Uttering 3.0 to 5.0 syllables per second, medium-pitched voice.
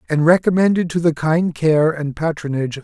No: 5.6 syllables/s; medium, 155 Hz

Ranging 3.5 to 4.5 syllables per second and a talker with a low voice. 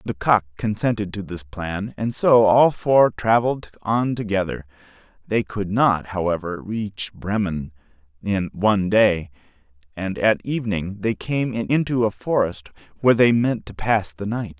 Yes: 4.3 syllables/s; low, 105 Hz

